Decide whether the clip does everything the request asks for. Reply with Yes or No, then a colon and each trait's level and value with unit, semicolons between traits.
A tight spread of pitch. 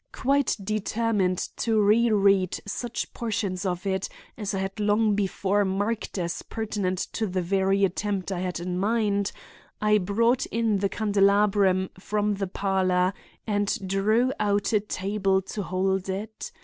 Yes: narrow, 1.9 semitones